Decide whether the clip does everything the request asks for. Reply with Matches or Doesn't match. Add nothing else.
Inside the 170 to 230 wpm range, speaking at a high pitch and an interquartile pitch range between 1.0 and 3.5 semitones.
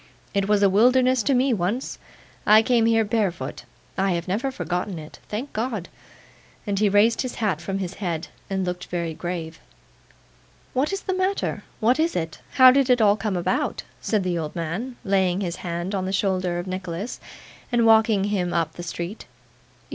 Doesn't match